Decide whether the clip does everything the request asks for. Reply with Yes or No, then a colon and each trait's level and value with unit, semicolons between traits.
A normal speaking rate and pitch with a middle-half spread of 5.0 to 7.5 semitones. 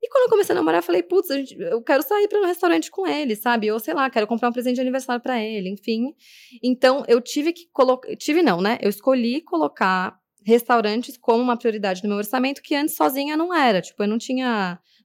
No: fast, 225 wpm; wide, 5.5 semitones